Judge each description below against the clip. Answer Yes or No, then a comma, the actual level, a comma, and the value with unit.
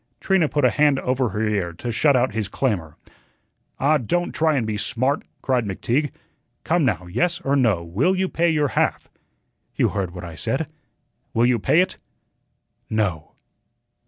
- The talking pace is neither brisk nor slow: Yes, average, 170 wpm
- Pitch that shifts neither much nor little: No, wide, 6.2 semitones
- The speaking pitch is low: Yes, low, 125 Hz